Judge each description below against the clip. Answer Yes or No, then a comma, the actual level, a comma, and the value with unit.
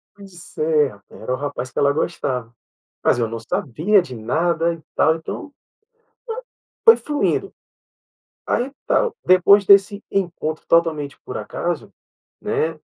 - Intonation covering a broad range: Yes, wide, 6.4 semitones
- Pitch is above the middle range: No, medium, 160 Hz